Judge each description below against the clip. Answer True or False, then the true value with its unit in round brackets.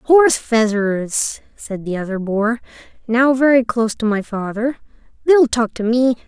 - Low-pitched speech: False (235 Hz)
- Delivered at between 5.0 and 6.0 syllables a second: False (4.8 syllables/s)